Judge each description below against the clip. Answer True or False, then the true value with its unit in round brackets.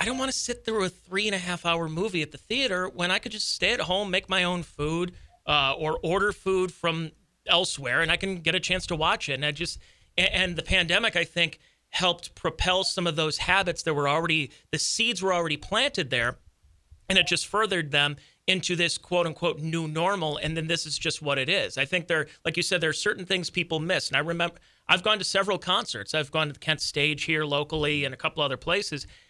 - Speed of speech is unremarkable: False (240 wpm)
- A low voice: False (170 Hz)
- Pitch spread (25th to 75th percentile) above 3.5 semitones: False (3.1 semitones)